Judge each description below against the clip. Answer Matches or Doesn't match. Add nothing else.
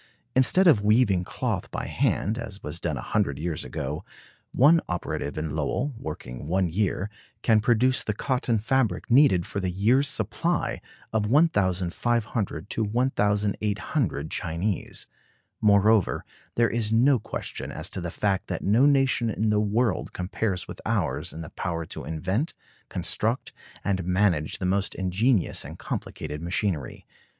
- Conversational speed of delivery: Matches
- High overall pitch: Doesn't match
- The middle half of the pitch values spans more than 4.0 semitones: Matches